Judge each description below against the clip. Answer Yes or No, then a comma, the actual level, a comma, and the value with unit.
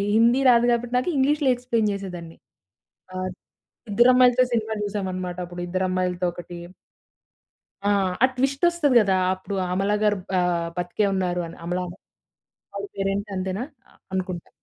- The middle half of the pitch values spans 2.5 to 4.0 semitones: No, average, 4.8 semitones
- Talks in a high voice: Yes, high, 195 Hz